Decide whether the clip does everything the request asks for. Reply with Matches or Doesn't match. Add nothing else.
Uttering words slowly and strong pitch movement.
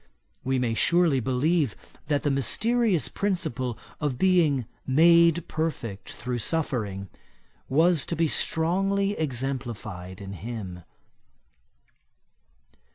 Matches